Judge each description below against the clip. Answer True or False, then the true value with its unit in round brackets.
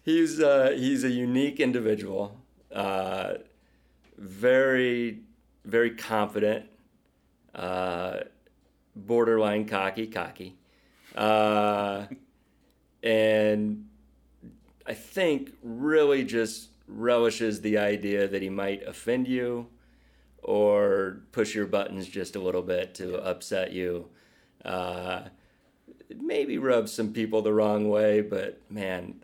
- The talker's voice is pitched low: True (110 Hz)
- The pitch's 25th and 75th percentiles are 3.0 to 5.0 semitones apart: True (3.7 semitones)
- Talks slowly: True (100 wpm)